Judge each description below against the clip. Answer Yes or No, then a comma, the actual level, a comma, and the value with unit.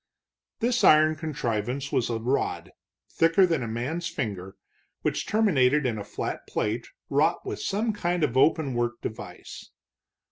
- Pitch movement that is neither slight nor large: No, wide, 5.9 semitones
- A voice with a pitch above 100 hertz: Yes, medium, 140 Hz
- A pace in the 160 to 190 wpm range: No, average, 150 wpm